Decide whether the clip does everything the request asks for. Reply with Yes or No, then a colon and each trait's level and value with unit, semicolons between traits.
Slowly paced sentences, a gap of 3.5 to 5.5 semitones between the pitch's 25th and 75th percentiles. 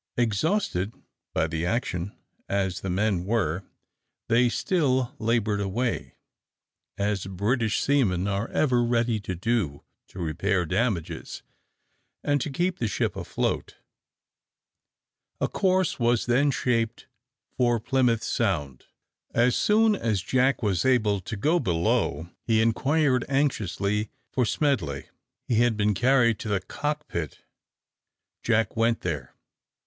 Yes: slow, 125 wpm; average, 4.7 semitones